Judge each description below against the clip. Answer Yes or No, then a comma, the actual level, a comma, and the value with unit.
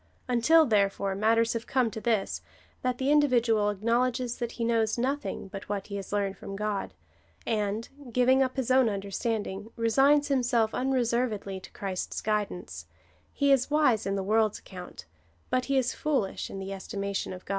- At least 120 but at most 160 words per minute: No, average, 175 wpm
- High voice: Yes, high, 225 Hz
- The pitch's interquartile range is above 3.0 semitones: Yes, average, 4.1 semitones